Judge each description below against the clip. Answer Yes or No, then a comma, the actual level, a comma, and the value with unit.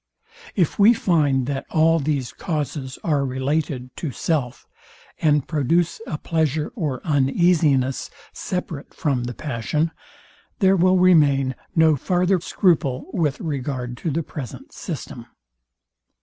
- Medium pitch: Yes, medium, 150 Hz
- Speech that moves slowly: Yes, slow, 120 wpm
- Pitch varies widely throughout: No, average, 3.8 semitones